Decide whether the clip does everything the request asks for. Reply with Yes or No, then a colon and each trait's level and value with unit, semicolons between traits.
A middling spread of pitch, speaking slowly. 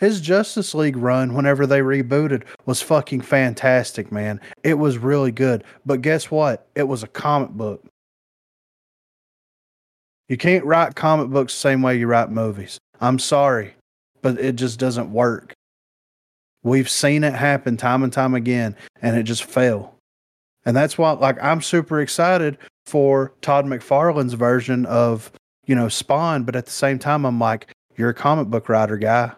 No: average, 3.2 semitones; average, 165 wpm